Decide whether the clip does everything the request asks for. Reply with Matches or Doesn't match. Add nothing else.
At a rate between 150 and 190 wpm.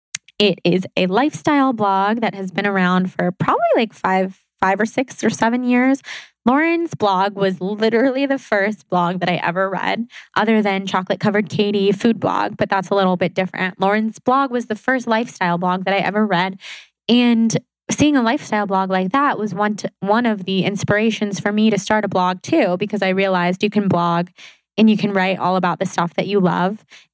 Doesn't match